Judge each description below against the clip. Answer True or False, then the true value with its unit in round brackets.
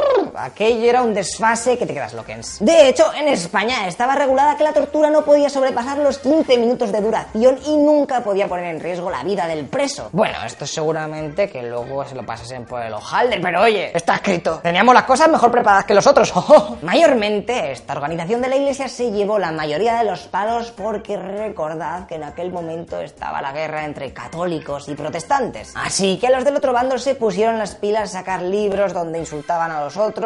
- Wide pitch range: True (7.5 semitones)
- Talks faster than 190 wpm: True (205 wpm)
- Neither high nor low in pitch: False (215 Hz)